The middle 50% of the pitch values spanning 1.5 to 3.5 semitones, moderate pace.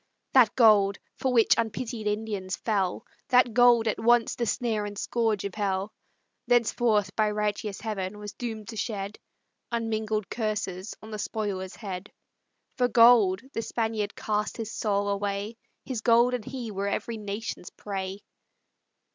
Yes: narrow, 2.4 semitones; average, 145 wpm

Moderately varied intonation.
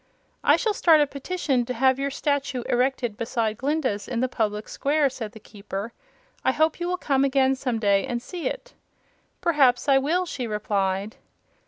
Yes: average, 4.4 semitones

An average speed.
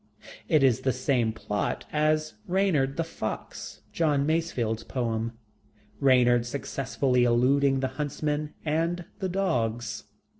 No: slow, 115 wpm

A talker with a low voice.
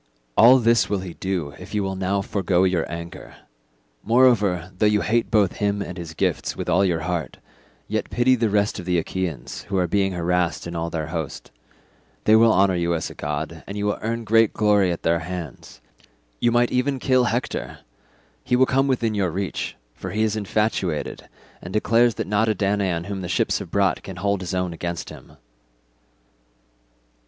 Yes: low, 100 Hz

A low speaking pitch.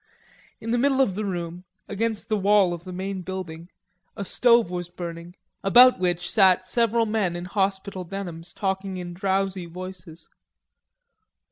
No: high, 190 Hz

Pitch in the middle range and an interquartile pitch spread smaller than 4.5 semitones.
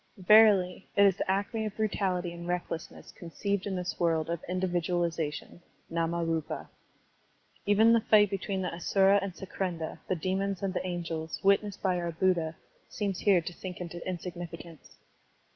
Yes: medium, 180 Hz; narrow, 2.6 semitones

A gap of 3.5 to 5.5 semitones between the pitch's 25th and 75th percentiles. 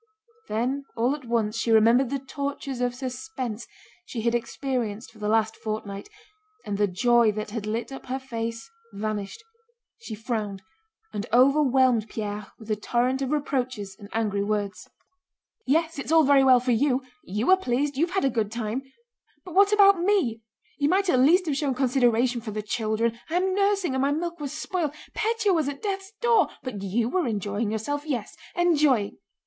Yes: average, 5.0 semitones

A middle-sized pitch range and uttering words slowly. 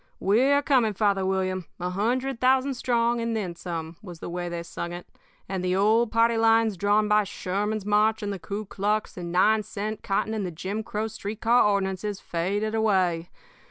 No: average, 3.0 semitones; average, 185 wpm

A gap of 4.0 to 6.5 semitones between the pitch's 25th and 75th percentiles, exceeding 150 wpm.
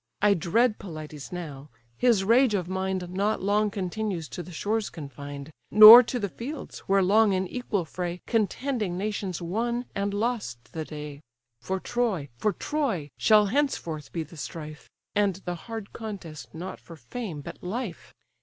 Yes: average, 4.9 semitones; average, 160 wpm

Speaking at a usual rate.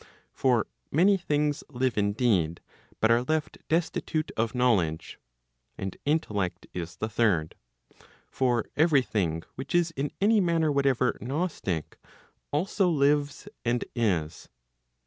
No: slow, 120 wpm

